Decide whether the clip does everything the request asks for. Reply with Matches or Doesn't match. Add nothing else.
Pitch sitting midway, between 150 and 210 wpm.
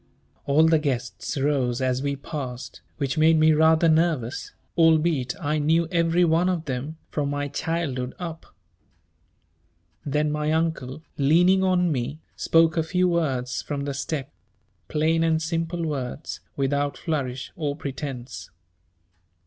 Doesn't match